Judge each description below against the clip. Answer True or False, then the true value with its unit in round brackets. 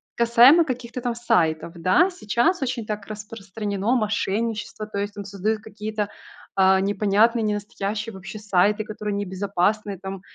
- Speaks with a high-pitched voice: True (210 Hz)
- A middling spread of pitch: False (2.3 semitones)